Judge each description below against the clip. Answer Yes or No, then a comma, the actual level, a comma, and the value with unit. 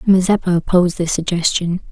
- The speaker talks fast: No, slow, 125 wpm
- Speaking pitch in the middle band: Yes, medium, 180 Hz